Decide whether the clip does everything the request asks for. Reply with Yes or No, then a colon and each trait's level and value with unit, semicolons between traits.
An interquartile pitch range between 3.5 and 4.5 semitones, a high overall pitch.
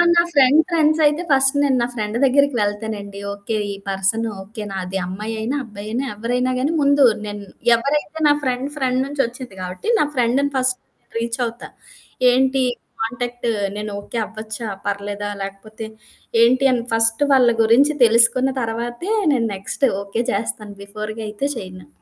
Yes: average, 4.0 semitones; high, 230 Hz